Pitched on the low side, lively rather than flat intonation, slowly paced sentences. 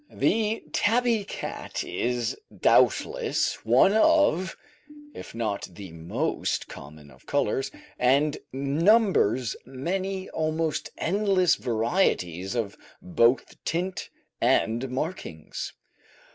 No: medium, 150 Hz; wide, 8.8 semitones; slow, 90 wpm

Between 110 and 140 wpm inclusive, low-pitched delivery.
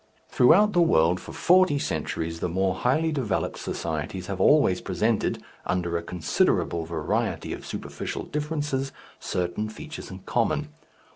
Yes: slow, 135 wpm; very low, 95 Hz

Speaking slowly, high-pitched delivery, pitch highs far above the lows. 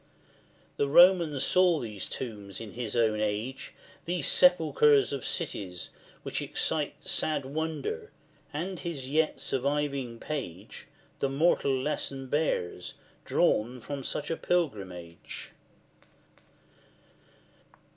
No: slow, 100 wpm; medium, 140 Hz; wide, 5.7 semitones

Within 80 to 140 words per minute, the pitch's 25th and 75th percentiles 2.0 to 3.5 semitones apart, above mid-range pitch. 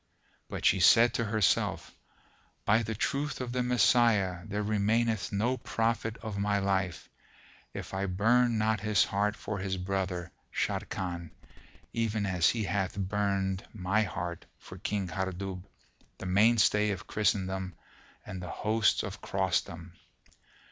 No: slow, 135 wpm; narrow, 2.6 semitones; low, 100 Hz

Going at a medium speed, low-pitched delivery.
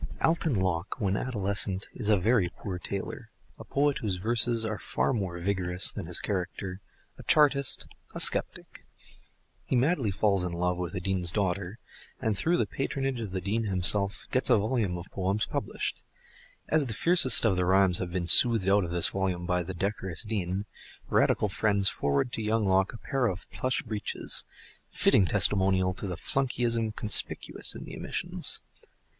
Yes: average, 170 wpm; low, 100 Hz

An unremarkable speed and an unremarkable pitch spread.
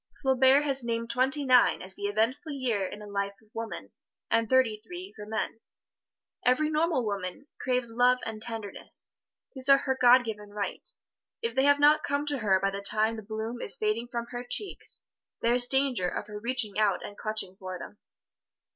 Yes: average, 190 wpm; average, 3.9 semitones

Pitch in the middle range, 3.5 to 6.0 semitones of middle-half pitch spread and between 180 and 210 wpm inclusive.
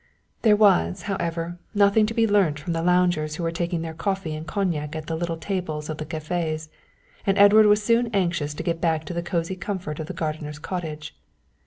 Yes: medium, 170 Hz; average, 3.9 semitones; fast, 205 wpm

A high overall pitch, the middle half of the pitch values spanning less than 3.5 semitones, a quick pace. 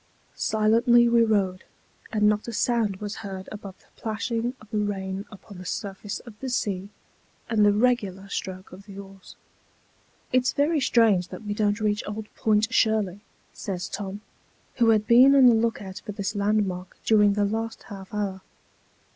No: high, 210 Hz; narrow, 2.5 semitones; average, 170 wpm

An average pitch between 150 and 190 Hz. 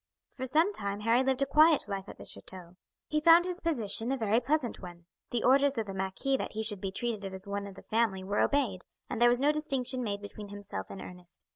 No: high, 225 Hz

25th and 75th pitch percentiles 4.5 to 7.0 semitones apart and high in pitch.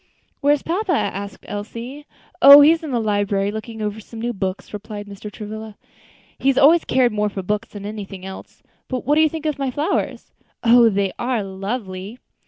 Yes: average, 4.9 semitones; high, 220 Hz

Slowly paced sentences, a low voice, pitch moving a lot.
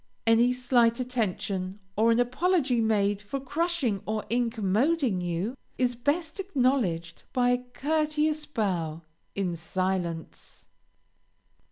No: slow, 110 wpm; high, 235 Hz; wide, 5.7 semitones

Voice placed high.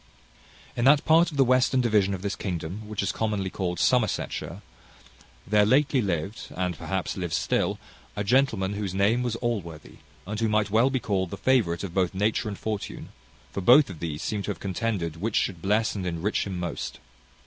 No: low, 105 Hz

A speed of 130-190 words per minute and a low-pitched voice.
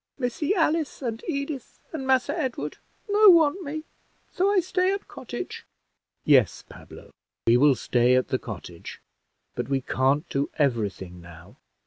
No: average, 150 wpm; high, 240 Hz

